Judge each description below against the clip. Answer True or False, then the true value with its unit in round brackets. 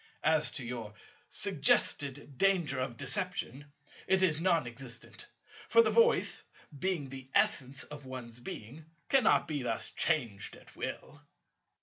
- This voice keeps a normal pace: False (130 wpm)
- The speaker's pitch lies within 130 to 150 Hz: True (140 Hz)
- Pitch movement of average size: True (5.0 semitones)